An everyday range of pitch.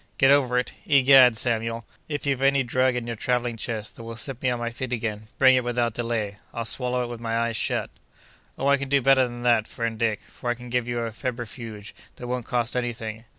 No: narrow, 1.7 semitones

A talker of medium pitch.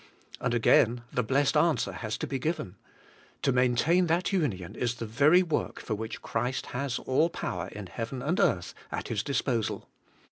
No: low, 125 Hz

